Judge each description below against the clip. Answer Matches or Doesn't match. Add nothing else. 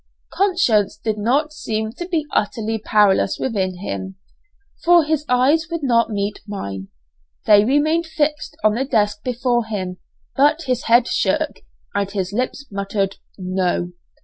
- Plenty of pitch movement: Matches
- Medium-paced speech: Matches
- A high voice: Matches